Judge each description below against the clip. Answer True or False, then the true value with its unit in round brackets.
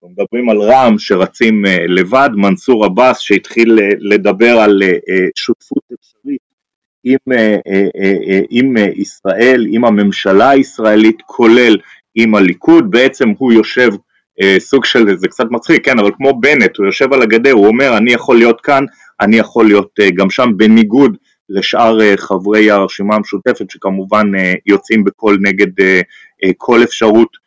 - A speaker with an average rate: True (130 wpm)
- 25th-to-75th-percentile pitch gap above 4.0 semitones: False (3.5 semitones)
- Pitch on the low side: True (110 Hz)